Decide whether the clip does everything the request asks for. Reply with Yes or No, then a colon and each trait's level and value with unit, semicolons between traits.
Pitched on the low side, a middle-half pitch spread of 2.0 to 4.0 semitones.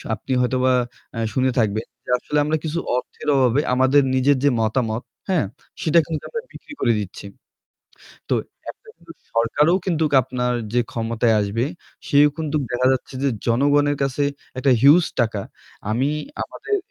Yes: low, 130 Hz; average, 3.7 semitones